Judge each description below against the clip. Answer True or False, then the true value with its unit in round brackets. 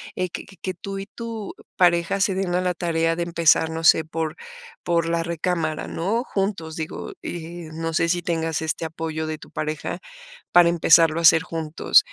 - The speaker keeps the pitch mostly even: True (1.8 semitones)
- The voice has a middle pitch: True (165 Hz)